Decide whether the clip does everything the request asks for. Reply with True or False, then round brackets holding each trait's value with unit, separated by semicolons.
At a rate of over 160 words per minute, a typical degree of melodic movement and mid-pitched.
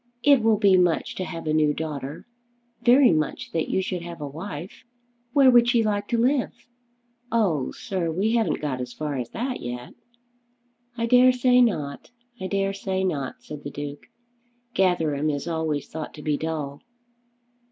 False (175 wpm; 6.9 semitones; 170 Hz)